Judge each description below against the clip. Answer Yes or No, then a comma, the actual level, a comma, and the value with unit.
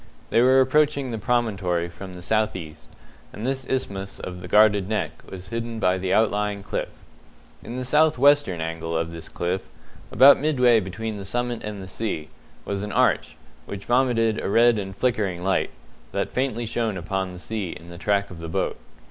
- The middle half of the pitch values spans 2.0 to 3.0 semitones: No, average, 4.7 semitones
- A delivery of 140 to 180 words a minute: No, average, 190 wpm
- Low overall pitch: Yes, low, 105 Hz